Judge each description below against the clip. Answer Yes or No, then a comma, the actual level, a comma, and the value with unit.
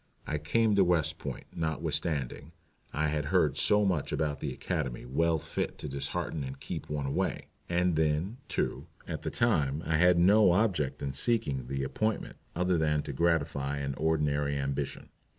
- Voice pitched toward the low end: Yes, very low, 75 Hz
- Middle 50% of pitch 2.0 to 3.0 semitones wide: No, average, 3.7 semitones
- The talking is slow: No, average, 170 wpm